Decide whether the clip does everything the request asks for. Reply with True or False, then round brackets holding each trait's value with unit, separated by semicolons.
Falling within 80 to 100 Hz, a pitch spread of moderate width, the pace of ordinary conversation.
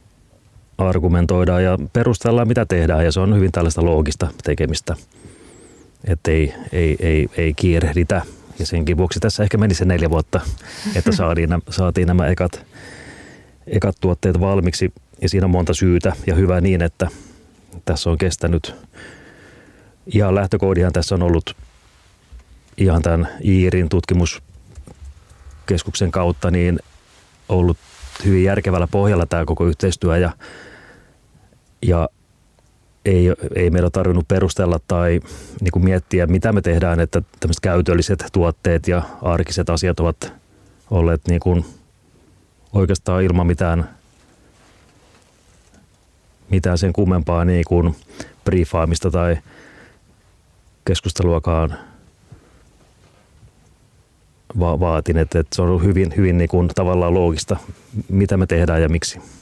False (90 Hz; 2.1 semitones; 120 wpm)